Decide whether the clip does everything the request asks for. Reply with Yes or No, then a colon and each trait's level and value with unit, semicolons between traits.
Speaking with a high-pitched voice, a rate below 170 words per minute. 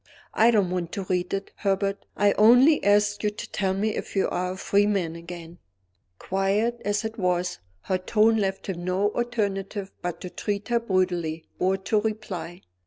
No: high, 195 Hz; average, 180 wpm